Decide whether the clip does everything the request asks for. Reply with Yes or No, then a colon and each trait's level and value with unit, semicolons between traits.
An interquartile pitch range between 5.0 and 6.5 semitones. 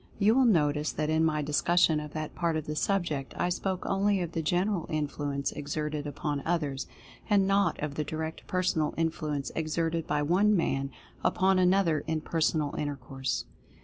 No: average, 3.2 semitones